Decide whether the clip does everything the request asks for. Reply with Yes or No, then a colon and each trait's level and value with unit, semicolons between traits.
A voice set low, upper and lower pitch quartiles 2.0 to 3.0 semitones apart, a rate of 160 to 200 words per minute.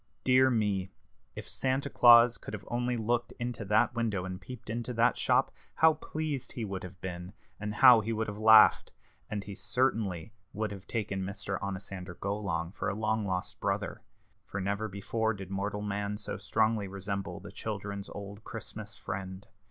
Yes: low, 105 Hz; average, 2.7 semitones; average, 175 wpm